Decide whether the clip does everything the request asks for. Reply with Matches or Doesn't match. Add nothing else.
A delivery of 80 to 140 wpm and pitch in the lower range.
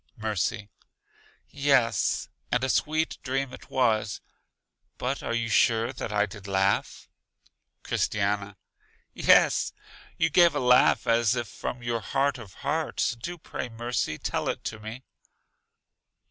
Matches